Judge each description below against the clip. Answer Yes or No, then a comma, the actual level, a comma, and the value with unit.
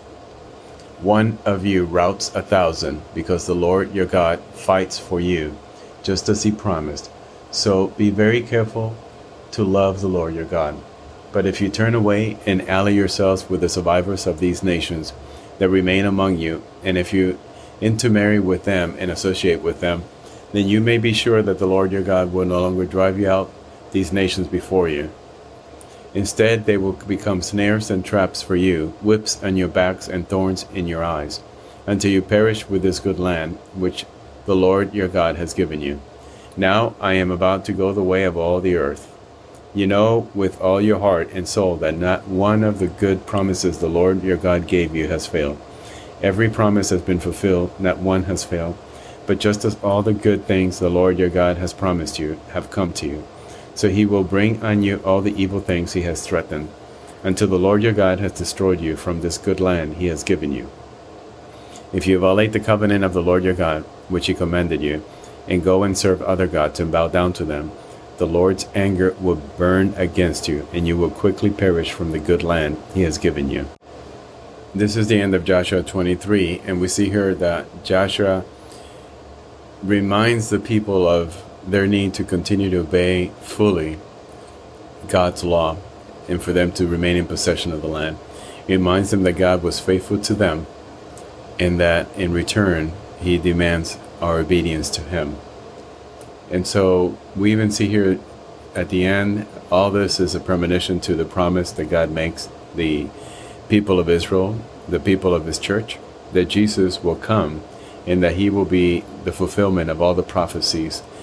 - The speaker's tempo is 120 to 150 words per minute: No, average, 185 wpm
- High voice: No, very low, 95 Hz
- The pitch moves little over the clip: Yes, narrow, 2.3 semitones